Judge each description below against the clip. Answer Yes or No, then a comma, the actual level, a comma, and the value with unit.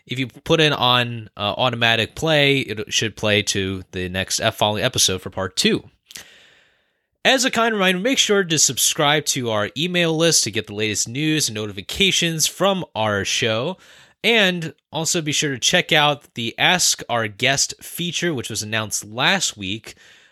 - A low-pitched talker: Yes, low, 130 Hz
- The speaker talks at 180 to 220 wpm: No, average, 170 wpm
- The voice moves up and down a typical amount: No, wide, 7.3 semitones